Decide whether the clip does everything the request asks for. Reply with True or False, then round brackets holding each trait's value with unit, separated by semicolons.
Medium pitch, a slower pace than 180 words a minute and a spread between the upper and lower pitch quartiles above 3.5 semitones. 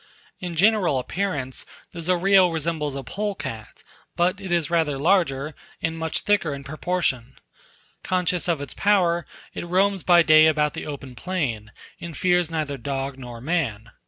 True (160 Hz; 155 wpm; 4.6 semitones)